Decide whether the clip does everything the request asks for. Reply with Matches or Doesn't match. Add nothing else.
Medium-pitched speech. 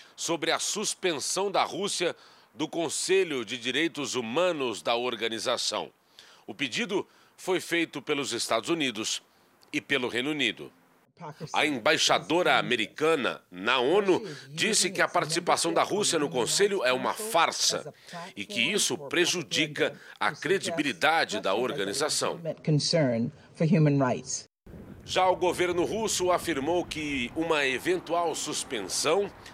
Matches